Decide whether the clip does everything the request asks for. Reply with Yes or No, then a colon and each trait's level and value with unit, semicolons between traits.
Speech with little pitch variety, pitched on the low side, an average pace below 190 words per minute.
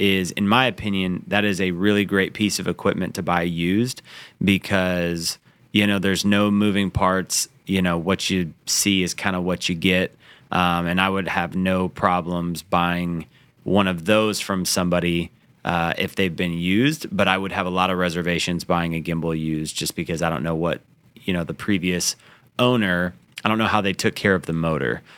No: narrow, 2.3 semitones; very low, 95 Hz; average, 200 wpm